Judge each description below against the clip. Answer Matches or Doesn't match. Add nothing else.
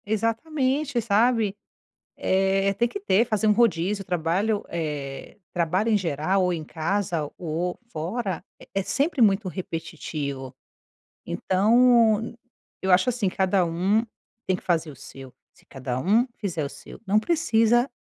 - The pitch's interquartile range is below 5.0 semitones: Doesn't match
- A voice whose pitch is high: Matches